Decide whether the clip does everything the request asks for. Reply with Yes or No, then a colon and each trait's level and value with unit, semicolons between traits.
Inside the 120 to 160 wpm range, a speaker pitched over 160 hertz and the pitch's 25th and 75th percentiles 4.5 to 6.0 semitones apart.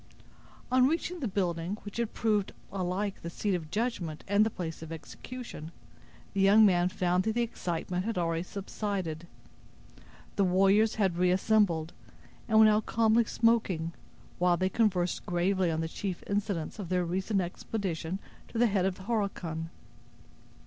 No: average, 155 wpm; high, 190 Hz; average, 3.6 semitones